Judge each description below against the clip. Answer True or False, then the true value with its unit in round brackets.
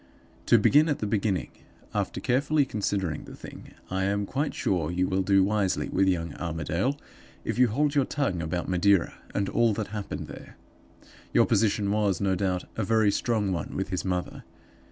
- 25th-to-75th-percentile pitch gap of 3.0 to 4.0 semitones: True (3.4 semitones)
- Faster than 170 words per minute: True (180 wpm)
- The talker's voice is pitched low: True (100 Hz)